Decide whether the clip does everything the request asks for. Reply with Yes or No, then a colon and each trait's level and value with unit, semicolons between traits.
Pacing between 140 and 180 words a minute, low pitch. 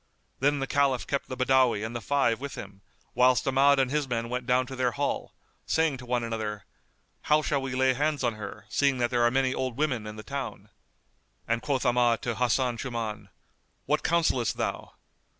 No: average, 200 wpm; low, 125 Hz